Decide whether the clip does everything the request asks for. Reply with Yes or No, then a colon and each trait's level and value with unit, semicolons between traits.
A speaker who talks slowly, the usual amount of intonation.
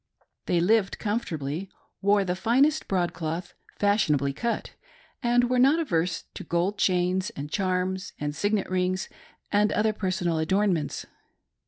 Yes: slow, 130 wpm; average, 3.5 semitones